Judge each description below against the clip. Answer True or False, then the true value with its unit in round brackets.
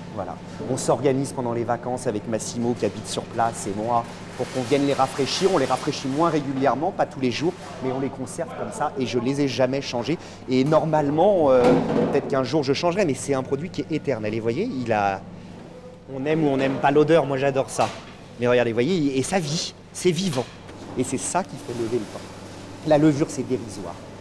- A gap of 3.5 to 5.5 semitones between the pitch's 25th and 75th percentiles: True (3.8 semitones)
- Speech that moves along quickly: True (230 wpm)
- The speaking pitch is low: True (130 Hz)